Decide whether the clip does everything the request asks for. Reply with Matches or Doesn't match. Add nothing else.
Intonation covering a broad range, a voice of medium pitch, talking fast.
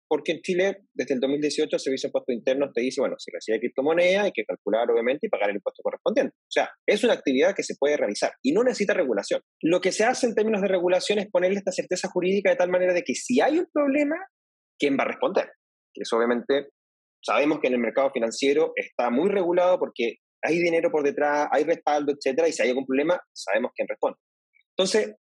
Matches